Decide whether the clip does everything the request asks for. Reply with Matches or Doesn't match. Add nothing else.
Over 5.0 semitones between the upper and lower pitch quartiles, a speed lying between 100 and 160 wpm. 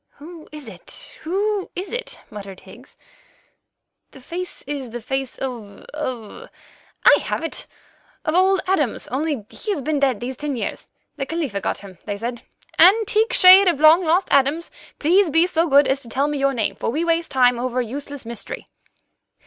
Doesn't match